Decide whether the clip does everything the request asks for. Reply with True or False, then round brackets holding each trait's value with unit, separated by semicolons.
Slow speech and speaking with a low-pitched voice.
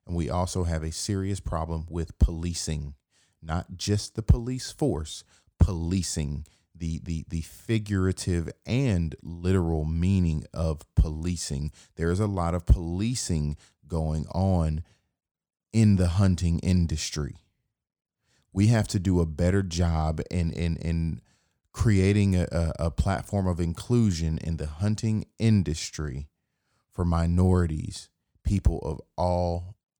True (120 wpm; 85 Hz)